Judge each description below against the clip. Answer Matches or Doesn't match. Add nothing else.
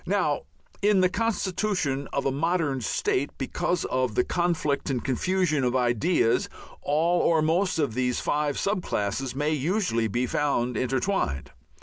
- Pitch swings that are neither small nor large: Doesn't match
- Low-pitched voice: Doesn't match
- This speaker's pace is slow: Doesn't match